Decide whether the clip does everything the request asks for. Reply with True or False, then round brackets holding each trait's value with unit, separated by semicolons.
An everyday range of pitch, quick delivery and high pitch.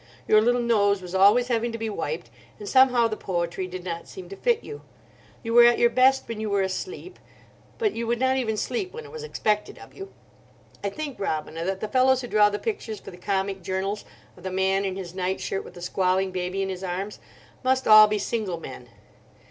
True (4.4 semitones; 225 wpm; 210 Hz)